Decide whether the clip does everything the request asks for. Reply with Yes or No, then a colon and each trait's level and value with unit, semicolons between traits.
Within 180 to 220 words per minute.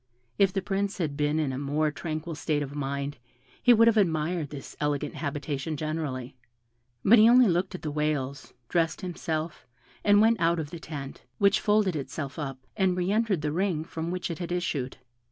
Yes: average, 190 wpm